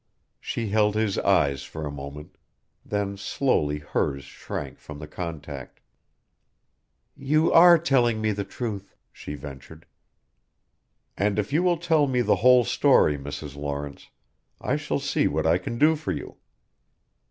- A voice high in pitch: No, low, 100 Hz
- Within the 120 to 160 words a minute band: Yes, average, 145 wpm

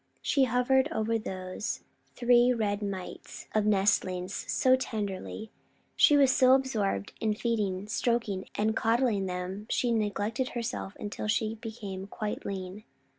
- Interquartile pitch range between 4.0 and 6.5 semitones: No, average, 3.4 semitones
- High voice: Yes, high, 215 Hz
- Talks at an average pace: No, slow, 130 wpm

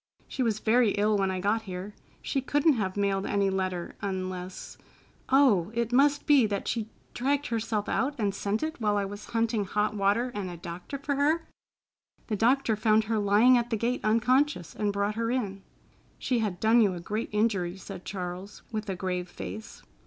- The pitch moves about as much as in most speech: Yes, average, 3.5 semitones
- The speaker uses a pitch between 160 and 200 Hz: No, high, 210 Hz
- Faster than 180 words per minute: Yes, average, 190 wpm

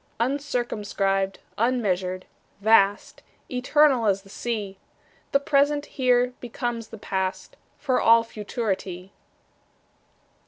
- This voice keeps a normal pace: No, slow, 90 wpm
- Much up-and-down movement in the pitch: No, average, 4.3 semitones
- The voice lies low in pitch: No, high, 230 Hz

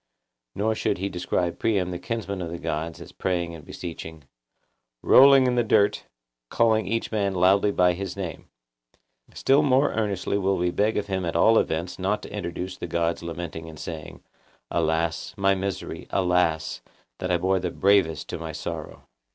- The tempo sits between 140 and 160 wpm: No, average, 175 wpm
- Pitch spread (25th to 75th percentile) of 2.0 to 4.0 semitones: Yes, average, 3.3 semitones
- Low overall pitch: Yes, very low, 90 Hz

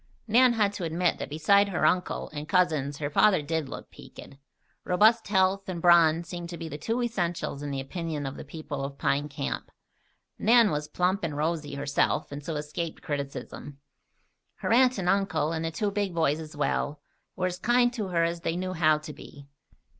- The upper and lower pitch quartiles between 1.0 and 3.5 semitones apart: No, average, 4.3 semitones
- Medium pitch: Yes, medium, 165 Hz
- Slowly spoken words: No, average, 200 wpm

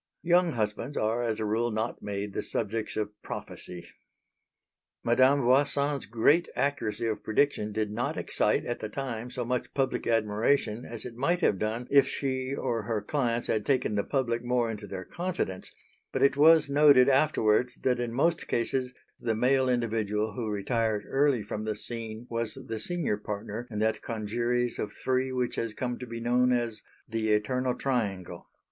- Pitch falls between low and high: No, low, 120 Hz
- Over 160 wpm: Yes, average, 175 wpm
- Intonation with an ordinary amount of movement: Yes, average, 3.3 semitones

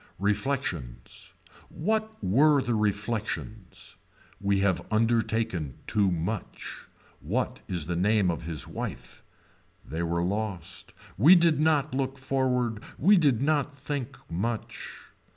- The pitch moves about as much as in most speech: No, wide, 6.7 semitones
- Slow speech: Yes, slow, 115 wpm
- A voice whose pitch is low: Yes, low, 110 Hz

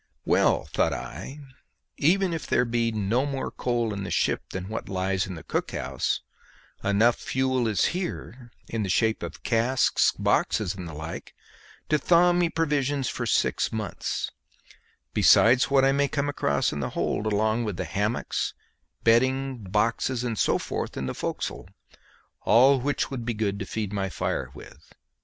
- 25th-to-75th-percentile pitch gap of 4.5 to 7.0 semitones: Yes, average, 4.9 semitones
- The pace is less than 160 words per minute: No, average, 170 wpm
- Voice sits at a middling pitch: No, low, 115 Hz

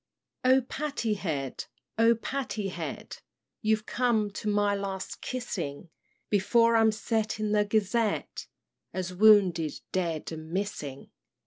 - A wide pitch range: No, average, 3.5 semitones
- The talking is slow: Yes, slow, 120 wpm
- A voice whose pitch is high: Yes, high, 210 Hz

